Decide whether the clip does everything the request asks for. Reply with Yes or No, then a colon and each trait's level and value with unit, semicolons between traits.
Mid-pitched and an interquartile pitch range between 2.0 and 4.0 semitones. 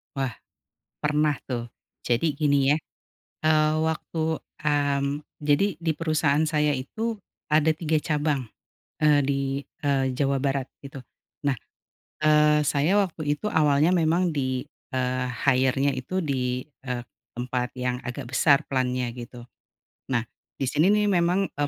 Yes: medium, 145 Hz; average, 2.9 semitones